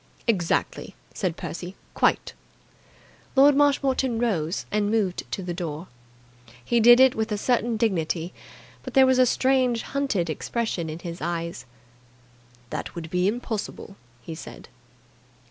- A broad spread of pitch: Yes, wide, 6.2 semitones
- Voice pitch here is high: Yes, high, 205 Hz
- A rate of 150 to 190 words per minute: No, slow, 135 wpm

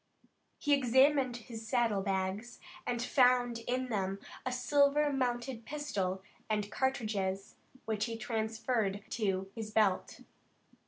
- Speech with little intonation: No, average, 3.7 semitones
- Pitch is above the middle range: Yes, high, 230 Hz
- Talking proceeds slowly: Yes, slow, 115 wpm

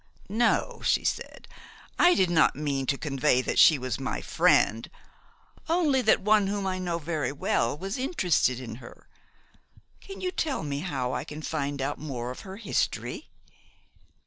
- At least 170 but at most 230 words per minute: No, average, 160 wpm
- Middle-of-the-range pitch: Yes, medium, 155 Hz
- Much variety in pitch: Yes, wide, 6.3 semitones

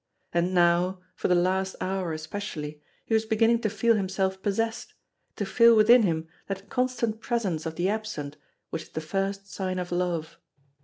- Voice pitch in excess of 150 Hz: Yes, high, 190 Hz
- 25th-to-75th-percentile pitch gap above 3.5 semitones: Yes, average, 3.9 semitones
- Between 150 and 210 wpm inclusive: Yes, average, 170 wpm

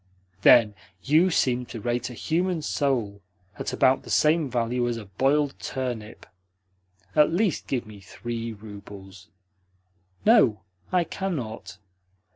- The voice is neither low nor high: No, low, 125 Hz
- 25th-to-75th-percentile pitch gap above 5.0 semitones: Yes, wide, 5.6 semitones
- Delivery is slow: Yes, slow, 125 wpm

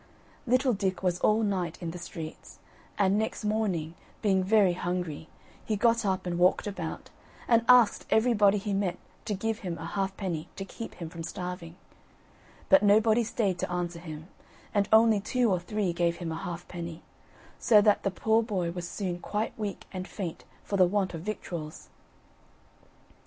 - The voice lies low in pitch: No, high, 190 Hz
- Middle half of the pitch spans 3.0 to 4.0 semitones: Yes, average, 3.5 semitones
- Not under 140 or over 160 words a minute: No, average, 170 wpm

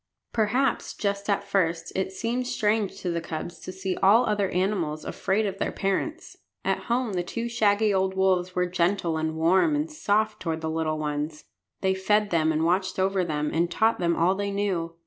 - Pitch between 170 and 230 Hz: Yes, high, 190 Hz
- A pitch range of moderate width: Yes, average, 3.7 semitones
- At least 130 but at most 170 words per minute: No, average, 195 wpm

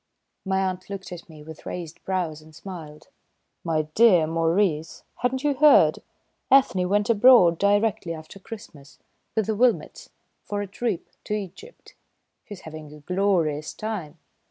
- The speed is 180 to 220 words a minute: No, average, 145 wpm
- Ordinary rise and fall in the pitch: Yes, average, 4.7 semitones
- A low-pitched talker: No, medium, 185 Hz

